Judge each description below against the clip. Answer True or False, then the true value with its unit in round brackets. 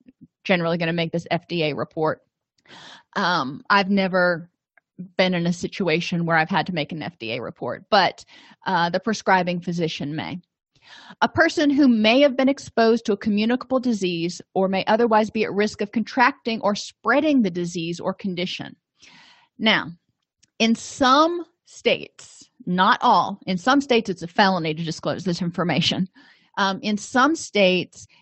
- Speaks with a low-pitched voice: False (195 Hz)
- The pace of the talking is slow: False (155 wpm)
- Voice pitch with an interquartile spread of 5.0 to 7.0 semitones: True (5.4 semitones)